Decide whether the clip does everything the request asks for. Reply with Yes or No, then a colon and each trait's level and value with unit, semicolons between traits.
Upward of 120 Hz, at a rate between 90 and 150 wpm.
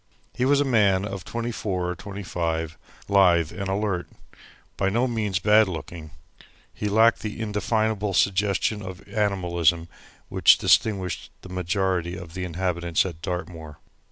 No: very low, 95 Hz; average, 145 wpm